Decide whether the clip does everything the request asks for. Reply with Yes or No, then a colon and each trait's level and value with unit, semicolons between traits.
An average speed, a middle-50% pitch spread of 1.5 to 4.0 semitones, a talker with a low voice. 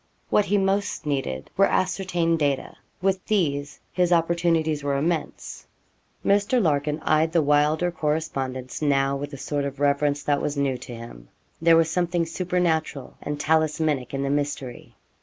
No: average, 155 wpm; average, 3.4 semitones; medium, 155 Hz